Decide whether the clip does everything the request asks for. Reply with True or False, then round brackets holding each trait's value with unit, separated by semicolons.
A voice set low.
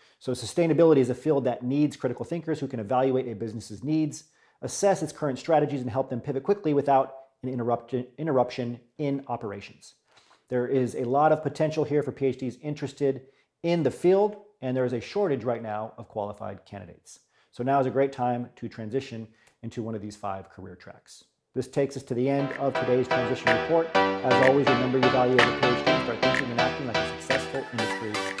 True (130 Hz)